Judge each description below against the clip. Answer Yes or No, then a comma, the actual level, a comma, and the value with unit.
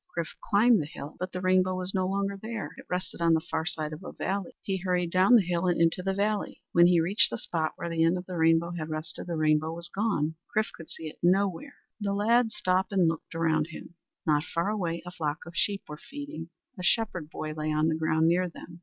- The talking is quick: Yes, fast, 240 wpm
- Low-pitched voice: No, medium, 175 Hz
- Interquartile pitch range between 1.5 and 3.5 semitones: Yes, average, 3.1 semitones